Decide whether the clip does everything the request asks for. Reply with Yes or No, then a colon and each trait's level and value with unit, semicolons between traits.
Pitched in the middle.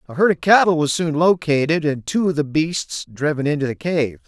Yes: medium, 155 Hz